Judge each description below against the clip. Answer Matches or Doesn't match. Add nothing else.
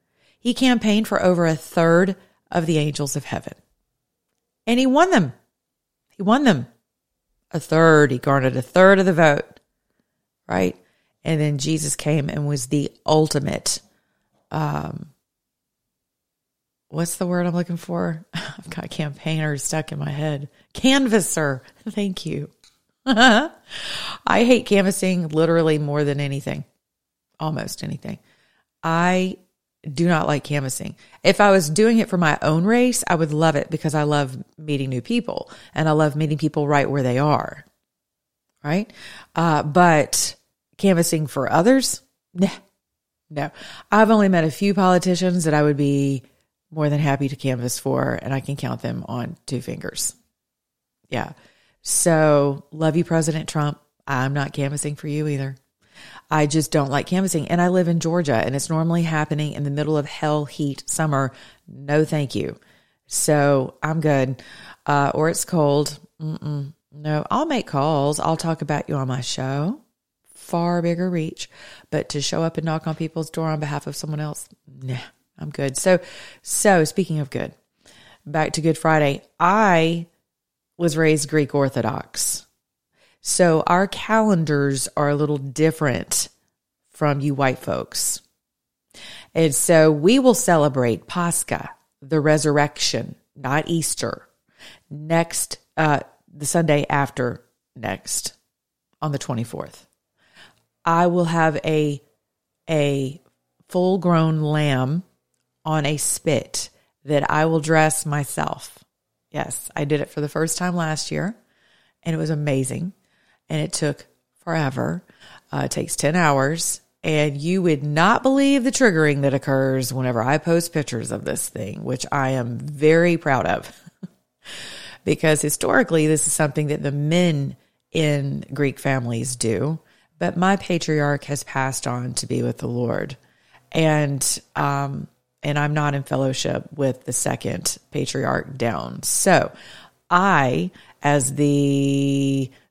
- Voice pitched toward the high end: Doesn't match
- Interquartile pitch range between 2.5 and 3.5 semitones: Matches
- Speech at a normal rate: Matches